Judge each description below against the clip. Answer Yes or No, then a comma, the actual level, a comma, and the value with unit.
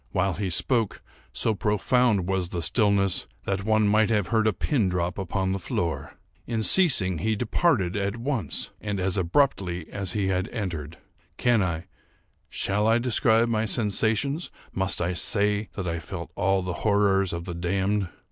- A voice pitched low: Yes, low, 100 Hz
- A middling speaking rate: Yes, average, 165 wpm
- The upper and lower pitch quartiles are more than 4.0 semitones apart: No, average, 3.3 semitones